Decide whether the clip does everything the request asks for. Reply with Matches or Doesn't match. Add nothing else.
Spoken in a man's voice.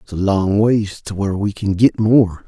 Matches